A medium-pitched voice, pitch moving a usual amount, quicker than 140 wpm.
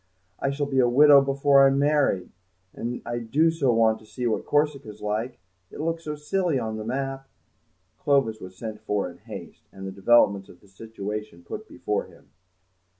No: low, 120 Hz; average, 4.7 semitones; average, 185 wpm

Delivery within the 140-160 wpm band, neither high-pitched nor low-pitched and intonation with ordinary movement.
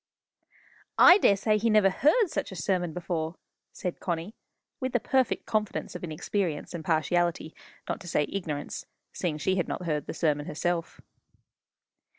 Yes: average, 155 wpm; medium, 175 Hz; average, 4.3 semitones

